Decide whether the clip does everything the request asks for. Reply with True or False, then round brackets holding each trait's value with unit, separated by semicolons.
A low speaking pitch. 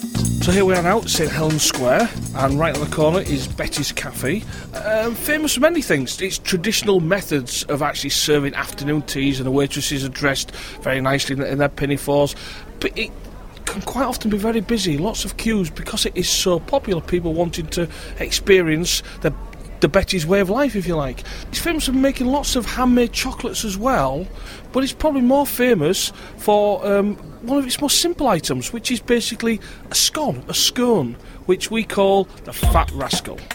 False (190 Hz)